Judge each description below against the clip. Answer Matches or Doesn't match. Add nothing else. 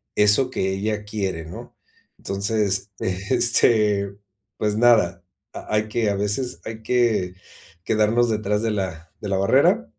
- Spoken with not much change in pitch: Matches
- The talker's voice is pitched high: Doesn't match